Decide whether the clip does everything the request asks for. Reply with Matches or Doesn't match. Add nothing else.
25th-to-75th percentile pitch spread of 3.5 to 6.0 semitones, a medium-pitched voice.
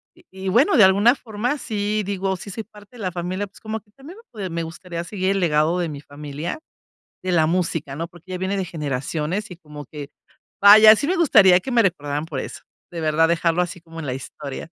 Matches